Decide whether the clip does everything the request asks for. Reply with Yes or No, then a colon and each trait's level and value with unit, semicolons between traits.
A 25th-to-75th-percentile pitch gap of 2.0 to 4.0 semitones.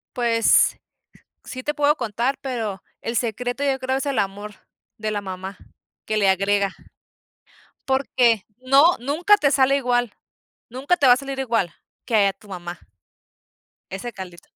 No: average, 4.9 semitones